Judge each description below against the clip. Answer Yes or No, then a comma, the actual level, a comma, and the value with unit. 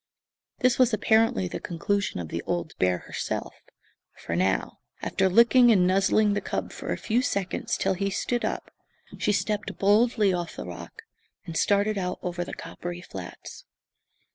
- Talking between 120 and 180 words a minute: Yes, average, 165 wpm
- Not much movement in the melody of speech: No, average, 3.8 semitones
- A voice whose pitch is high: Yes, high, 195 Hz